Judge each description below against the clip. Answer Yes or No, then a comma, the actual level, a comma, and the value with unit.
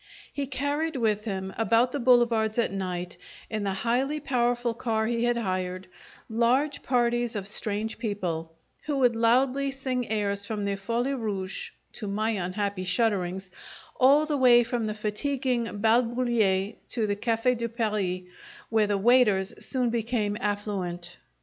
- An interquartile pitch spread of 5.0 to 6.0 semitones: No, average, 3.4 semitones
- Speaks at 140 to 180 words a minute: Yes, average, 150 wpm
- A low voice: No, high, 225 Hz